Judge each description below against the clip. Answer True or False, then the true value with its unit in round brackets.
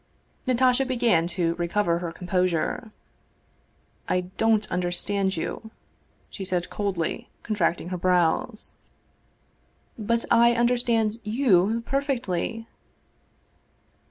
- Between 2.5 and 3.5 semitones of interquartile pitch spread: False (4.7 semitones)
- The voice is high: True (205 Hz)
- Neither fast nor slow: False (100 wpm)